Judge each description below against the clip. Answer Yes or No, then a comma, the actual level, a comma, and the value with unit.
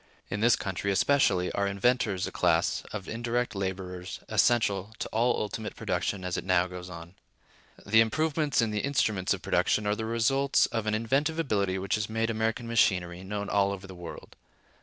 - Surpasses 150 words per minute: Yes, average, 180 wpm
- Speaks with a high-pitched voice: No, low, 105 Hz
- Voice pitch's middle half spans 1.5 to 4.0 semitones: Yes, average, 3.7 semitones